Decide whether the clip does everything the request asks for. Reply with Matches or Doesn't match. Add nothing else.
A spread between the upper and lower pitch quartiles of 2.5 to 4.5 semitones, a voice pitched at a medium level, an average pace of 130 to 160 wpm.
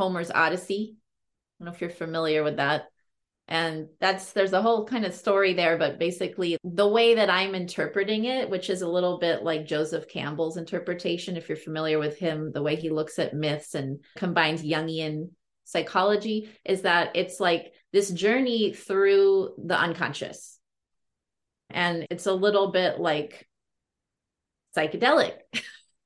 Matches